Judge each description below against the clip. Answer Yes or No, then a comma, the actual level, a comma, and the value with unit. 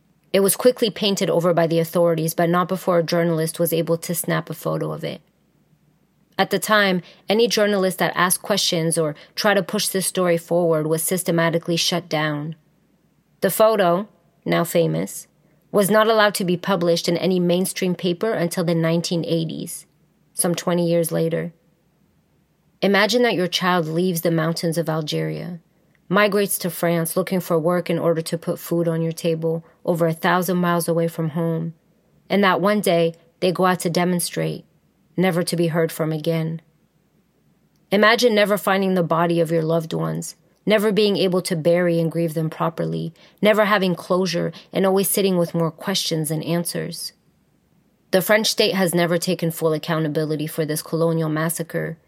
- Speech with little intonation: Yes, narrow, 2.2 semitones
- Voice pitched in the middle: Yes, medium, 170 Hz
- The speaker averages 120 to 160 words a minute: No, average, 170 wpm